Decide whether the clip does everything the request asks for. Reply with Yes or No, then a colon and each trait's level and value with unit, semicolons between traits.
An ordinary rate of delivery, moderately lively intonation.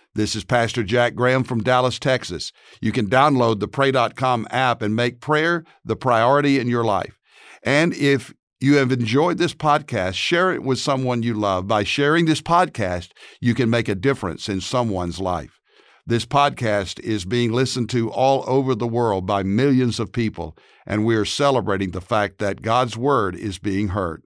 Yes: average, 180 wpm; average, 4.2 semitones